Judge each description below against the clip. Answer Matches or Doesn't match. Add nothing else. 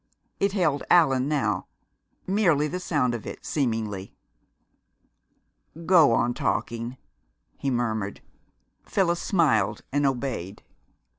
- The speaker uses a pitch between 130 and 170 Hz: Matches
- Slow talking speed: Matches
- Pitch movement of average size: Doesn't match